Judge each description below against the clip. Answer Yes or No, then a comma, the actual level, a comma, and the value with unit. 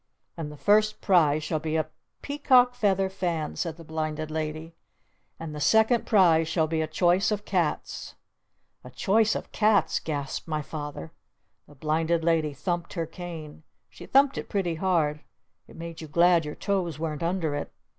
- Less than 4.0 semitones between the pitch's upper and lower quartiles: Yes, average, 3.6 semitones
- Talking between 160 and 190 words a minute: Yes, average, 170 wpm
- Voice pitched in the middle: Yes, medium, 165 Hz